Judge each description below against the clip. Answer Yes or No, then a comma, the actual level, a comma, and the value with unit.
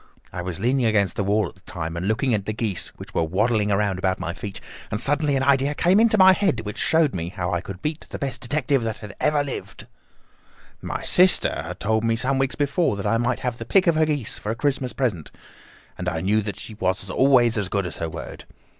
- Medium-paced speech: No, fast, 240 wpm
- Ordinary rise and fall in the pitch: No, wide, 6.1 semitones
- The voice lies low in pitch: Yes, low, 110 Hz